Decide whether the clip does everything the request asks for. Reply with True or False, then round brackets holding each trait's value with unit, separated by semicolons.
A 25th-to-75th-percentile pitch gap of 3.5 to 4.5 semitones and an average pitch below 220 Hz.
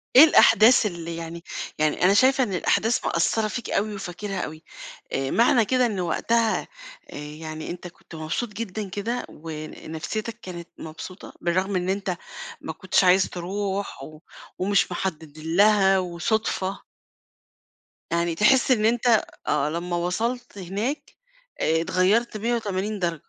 True (4.2 semitones; 190 Hz)